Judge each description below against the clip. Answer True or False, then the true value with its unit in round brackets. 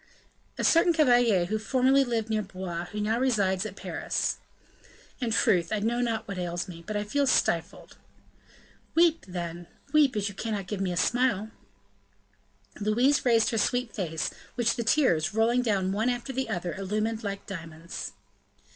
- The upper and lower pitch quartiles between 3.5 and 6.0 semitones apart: True (4.5 semitones)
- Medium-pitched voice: False (215 Hz)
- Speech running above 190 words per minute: False (170 wpm)